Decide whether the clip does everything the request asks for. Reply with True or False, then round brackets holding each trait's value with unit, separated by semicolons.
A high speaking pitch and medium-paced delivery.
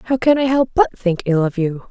False (220 Hz; 285 wpm)